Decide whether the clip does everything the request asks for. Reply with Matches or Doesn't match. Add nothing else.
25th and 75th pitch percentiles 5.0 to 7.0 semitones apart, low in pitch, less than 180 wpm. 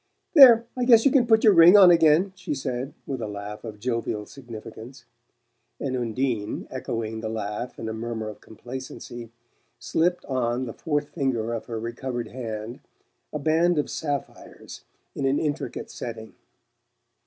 Matches